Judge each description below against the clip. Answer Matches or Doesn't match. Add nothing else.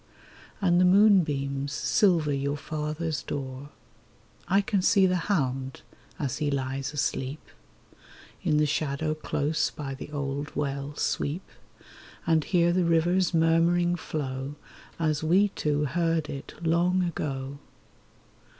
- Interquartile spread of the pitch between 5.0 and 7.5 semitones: Doesn't match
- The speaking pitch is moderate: Matches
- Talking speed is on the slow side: Matches